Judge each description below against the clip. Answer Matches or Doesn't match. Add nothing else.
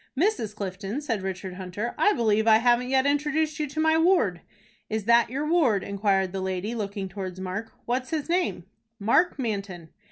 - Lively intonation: Matches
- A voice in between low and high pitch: Doesn't match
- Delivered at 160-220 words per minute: Matches